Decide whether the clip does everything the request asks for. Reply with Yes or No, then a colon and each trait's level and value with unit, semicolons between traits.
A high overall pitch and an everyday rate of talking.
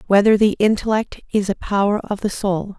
Yes: high, 205 Hz; average, 195 wpm